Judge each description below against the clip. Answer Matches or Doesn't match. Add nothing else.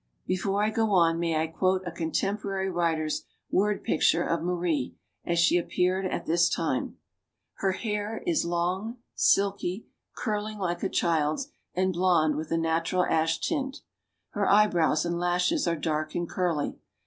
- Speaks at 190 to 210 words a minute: Doesn't match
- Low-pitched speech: Doesn't match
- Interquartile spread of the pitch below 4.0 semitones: Matches